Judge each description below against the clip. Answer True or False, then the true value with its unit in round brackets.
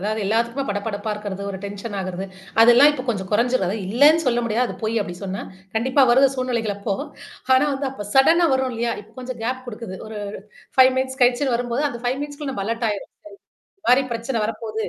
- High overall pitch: True (235 Hz)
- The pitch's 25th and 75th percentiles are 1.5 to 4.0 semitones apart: True (3.7 semitones)